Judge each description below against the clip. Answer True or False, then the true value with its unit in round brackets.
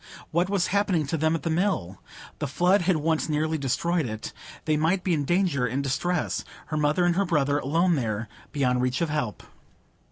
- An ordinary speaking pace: True (190 wpm)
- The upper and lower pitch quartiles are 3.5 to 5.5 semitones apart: True (4.1 semitones)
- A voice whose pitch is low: False (155 Hz)